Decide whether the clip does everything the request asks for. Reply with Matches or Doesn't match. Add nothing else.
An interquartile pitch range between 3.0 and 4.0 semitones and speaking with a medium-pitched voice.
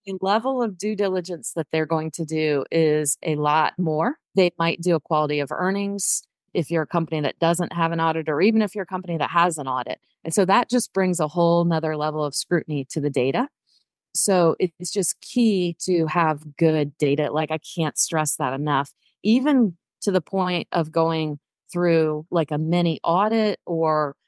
Matches